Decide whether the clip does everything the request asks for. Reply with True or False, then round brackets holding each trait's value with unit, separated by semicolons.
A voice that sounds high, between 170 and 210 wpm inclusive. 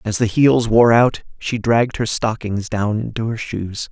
False (110 Hz; 200 wpm)